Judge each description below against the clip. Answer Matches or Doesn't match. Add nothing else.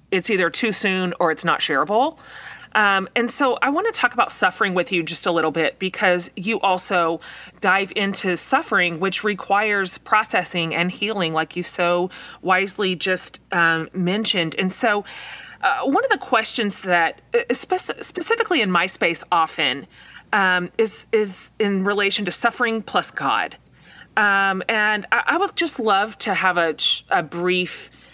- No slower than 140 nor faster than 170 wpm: Matches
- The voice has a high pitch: Matches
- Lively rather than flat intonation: Doesn't match